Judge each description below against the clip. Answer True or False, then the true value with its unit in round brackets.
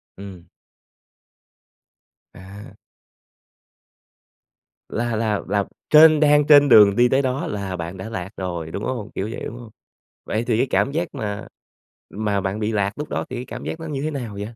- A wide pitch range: False (5.0 semitones)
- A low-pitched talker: True (110 Hz)